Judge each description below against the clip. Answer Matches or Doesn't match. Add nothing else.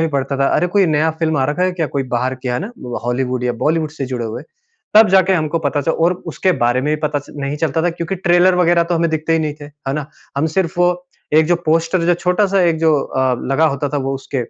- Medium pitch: Matches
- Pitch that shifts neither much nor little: Matches